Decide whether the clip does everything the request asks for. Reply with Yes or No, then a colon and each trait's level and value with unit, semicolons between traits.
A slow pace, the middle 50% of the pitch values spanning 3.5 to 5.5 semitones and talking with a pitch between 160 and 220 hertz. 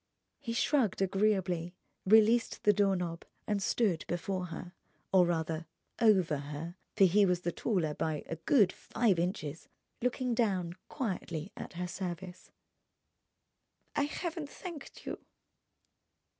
Yes: slow, 120 wpm; average, 4.2 semitones; medium, 185 Hz